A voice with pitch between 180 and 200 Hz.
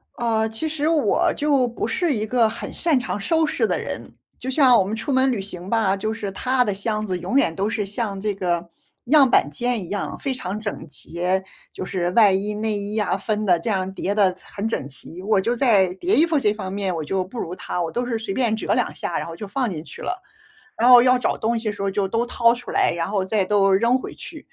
No: high, 215 Hz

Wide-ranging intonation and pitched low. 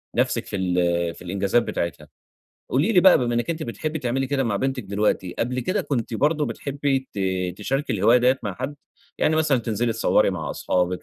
Yes: wide, 6.0 semitones; low, 120 Hz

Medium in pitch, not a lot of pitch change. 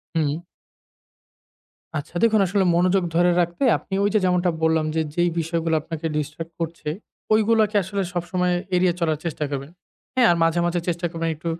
Yes: medium, 175 Hz; narrow, 2.0 semitones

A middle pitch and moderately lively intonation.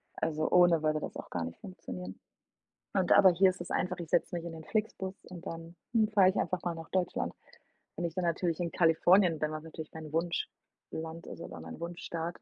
No: medium, 170 Hz; narrow, 2.2 semitones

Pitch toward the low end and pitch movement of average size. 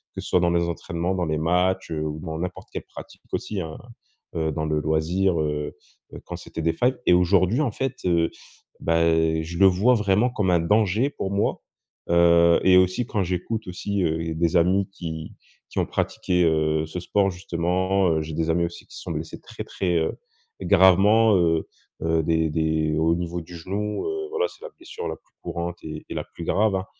Yes: very low, 90 Hz; average, 3.1 semitones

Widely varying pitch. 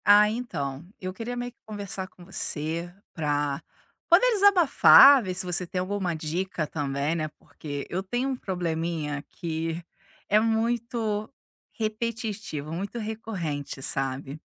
Yes: wide, 6.0 semitones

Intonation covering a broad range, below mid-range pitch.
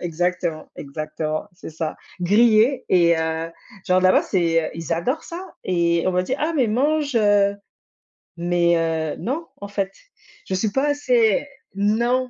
No: wide, 6.1 semitones; medium, 185 Hz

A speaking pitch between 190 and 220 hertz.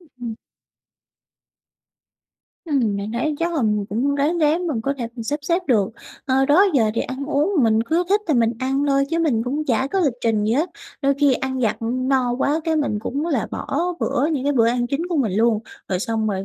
No: very high, 270 Hz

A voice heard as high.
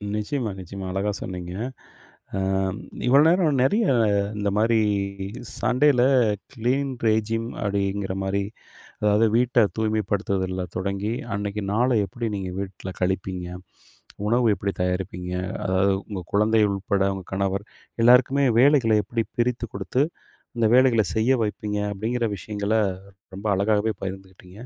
No: low, 105 Hz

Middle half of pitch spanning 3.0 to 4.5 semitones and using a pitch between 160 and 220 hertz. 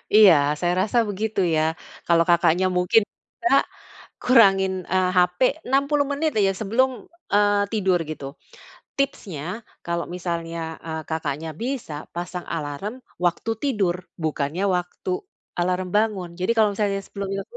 Yes: average, 4.0 semitones; high, 190 Hz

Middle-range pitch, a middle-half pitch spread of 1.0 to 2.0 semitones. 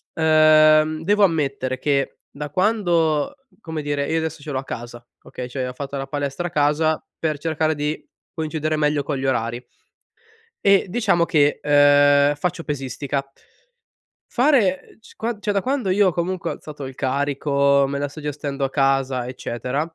No: medium, 150 Hz; average, 2.8 semitones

